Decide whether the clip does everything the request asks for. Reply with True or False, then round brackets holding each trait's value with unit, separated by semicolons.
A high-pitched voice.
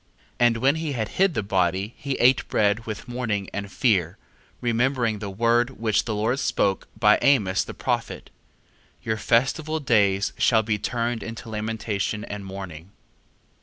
False (110 Hz)